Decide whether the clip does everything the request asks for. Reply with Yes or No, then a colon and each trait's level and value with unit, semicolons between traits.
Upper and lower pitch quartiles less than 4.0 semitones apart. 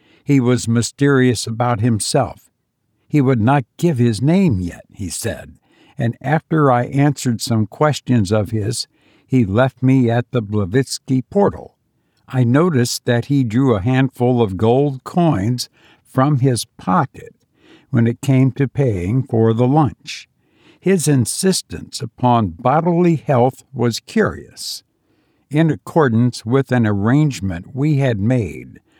Yes: average, 3.4 semitones